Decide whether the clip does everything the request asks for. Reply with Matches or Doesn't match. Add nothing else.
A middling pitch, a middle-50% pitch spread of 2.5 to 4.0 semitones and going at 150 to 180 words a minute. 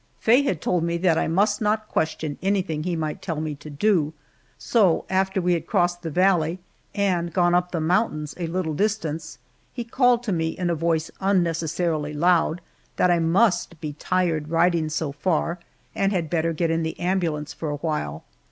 Doesn't match